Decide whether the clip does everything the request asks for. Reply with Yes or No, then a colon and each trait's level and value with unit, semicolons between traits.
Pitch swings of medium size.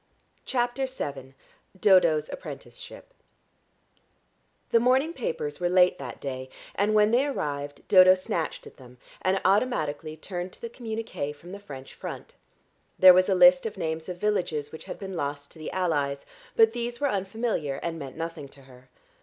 No: wide, 7.2 semitones